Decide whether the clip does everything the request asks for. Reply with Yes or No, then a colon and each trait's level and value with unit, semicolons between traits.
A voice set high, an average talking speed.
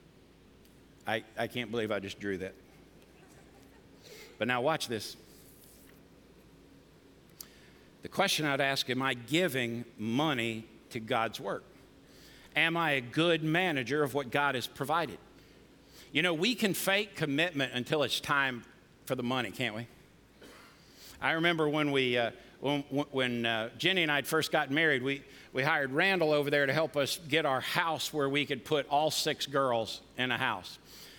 No: medium, 140 Hz; average, 160 wpm